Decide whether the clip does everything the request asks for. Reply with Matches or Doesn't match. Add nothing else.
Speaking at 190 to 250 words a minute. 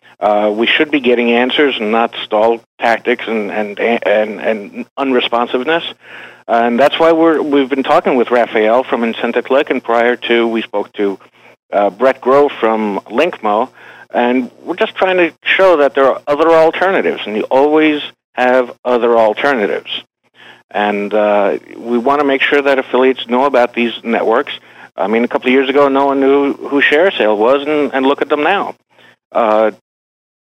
Doesn't match